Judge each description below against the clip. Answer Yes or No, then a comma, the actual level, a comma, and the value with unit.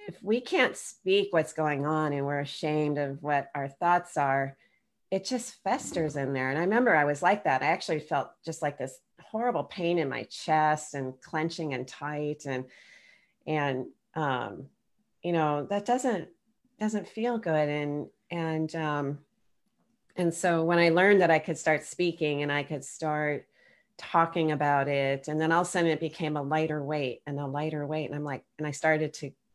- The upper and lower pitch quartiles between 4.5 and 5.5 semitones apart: No, average, 3.0 semitones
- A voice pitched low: No, medium, 155 Hz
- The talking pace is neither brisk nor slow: Yes, average, 190 wpm